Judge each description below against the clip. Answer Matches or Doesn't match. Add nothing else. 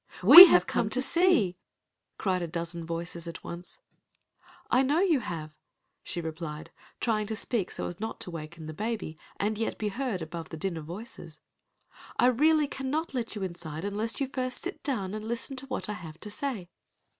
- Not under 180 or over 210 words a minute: Matches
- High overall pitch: Matches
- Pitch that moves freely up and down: Matches